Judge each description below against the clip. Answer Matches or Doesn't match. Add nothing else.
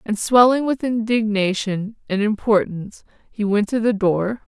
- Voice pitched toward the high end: Matches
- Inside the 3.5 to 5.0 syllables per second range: Matches